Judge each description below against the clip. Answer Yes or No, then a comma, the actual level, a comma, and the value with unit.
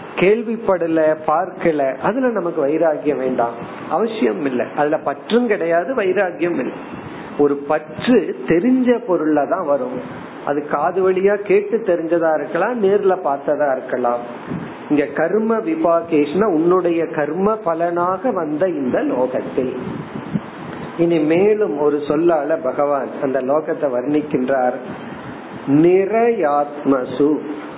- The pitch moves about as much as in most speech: Yes, average, 4.5 semitones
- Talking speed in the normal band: Yes, average, 95 wpm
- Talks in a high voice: No, medium, 160 Hz